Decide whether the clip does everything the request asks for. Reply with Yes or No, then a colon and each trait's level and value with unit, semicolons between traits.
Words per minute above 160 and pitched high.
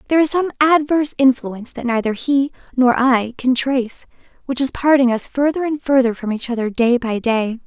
Yes: average, 195 wpm; very high, 255 Hz